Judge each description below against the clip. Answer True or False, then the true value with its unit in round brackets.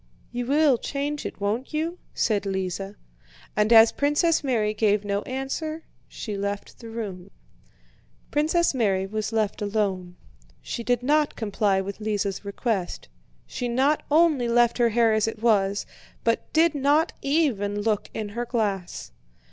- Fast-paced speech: False (150 wpm)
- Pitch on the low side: False (225 Hz)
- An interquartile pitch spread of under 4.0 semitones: False (5.1 semitones)